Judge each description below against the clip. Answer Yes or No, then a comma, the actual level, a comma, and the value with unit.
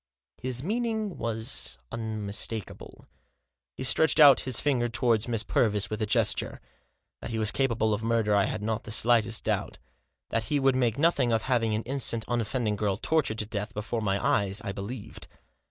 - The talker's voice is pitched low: Yes, low, 115 Hz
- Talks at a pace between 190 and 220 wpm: No, average, 175 wpm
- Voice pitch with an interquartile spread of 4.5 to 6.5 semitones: No, average, 3.1 semitones